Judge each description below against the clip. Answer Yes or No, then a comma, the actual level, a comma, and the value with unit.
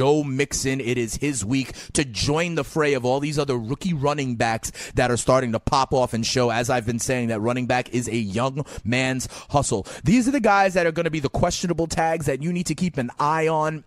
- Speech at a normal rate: No, fast, 245 wpm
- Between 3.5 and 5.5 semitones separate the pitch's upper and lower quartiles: Yes, average, 4.3 semitones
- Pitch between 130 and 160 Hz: Yes, low, 135 Hz